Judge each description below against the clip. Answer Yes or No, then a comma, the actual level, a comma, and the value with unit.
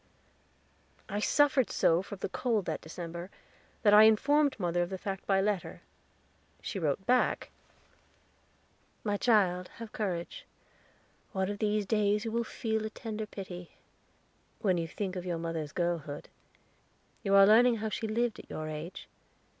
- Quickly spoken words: No, average, 155 wpm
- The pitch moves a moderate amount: Yes, average, 3.7 semitones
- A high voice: Yes, high, 200 Hz